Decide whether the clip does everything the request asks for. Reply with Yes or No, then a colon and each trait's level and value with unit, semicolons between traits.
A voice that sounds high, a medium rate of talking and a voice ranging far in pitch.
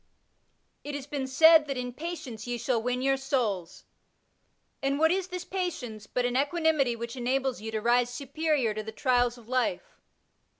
No: very high, 255 Hz; average, 180 wpm; average, 3.6 semitones